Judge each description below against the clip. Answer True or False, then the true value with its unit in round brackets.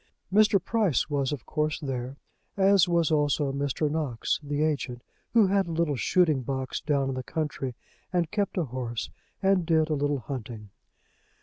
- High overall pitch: False (150 Hz)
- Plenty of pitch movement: False (4.2 semitones)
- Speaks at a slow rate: False (170 wpm)